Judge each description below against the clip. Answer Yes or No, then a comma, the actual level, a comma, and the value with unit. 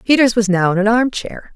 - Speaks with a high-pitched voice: Yes, high, 220 Hz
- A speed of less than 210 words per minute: No, fast, 270 wpm